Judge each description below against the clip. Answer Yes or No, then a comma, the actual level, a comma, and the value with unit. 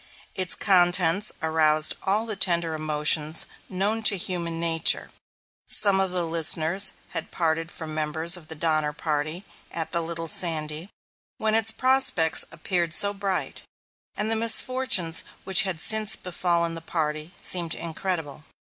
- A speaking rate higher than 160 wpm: No, average, 140 wpm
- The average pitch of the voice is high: No, medium, 170 Hz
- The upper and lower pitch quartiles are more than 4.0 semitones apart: No, average, 3.2 semitones